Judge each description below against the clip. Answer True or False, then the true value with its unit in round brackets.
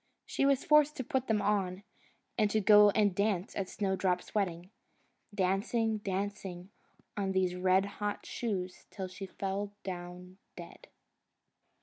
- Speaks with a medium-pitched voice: False (195 Hz)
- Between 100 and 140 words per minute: True (135 wpm)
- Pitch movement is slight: True (2.2 semitones)